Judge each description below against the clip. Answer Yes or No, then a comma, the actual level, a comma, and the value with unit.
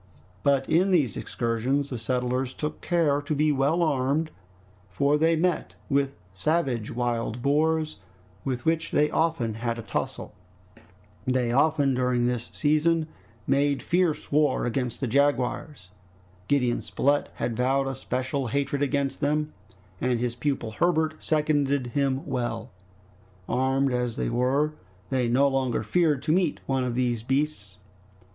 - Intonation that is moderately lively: Yes, average, 3.5 semitones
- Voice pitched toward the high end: No, low, 135 Hz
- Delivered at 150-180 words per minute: No, average, 140 wpm